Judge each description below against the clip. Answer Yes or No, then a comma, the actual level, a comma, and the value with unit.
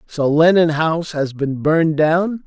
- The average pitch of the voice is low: No, medium, 160 Hz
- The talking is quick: No, average, 170 wpm